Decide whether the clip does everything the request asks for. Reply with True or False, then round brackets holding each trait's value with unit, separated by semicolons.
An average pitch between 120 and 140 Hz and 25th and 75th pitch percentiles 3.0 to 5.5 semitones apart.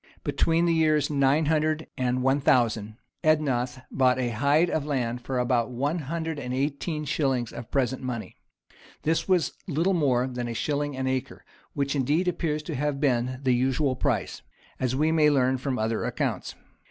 True (135 Hz; 3.4 semitones)